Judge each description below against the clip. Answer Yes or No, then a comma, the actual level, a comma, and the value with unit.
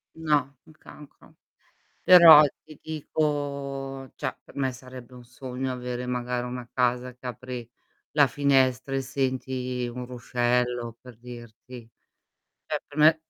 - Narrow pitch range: Yes, narrow, 2.1 semitones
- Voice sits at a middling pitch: No, low, 130 Hz